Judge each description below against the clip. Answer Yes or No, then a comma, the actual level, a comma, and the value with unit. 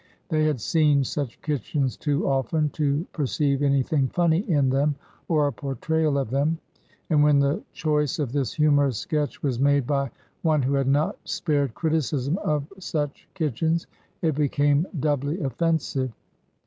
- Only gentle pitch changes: Yes, narrow, 2.0 semitones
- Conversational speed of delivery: Yes, average, 155 wpm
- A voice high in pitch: No, medium, 145 Hz